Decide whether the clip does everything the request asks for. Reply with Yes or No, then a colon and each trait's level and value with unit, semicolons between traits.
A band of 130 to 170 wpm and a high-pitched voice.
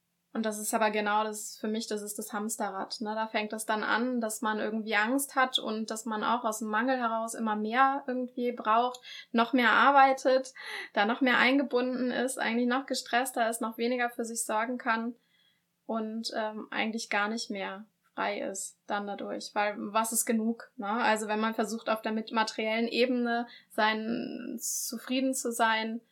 No: average, 185 wpm; high, 225 Hz